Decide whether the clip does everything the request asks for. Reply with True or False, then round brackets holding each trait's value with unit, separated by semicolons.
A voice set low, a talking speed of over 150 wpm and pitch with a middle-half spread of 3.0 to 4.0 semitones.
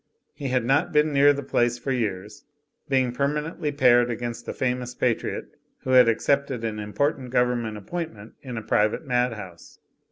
True (125 Hz; 160 wpm; 3.3 semitones)